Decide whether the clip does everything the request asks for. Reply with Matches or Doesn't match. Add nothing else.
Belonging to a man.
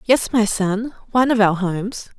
Doesn't match